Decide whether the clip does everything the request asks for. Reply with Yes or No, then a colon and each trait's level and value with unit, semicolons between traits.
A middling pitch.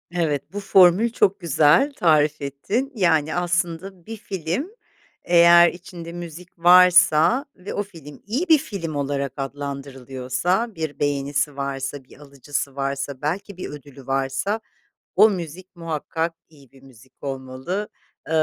Yes: medium, 160 Hz